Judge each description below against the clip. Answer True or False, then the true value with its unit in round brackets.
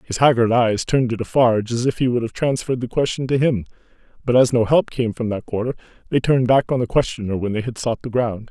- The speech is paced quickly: True (255 wpm)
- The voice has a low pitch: True (120 Hz)